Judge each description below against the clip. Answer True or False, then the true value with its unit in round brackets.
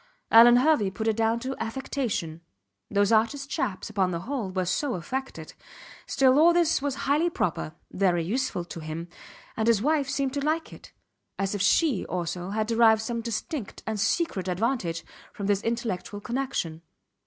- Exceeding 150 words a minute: True (165 wpm)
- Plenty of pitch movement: True (6.0 semitones)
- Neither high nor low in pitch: False (225 Hz)